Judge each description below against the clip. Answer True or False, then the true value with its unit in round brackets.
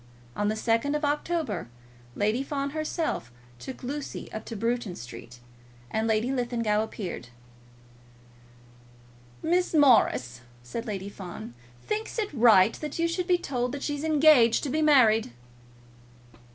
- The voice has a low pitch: False (245 Hz)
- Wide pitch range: True (5.9 semitones)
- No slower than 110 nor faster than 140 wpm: True (135 wpm)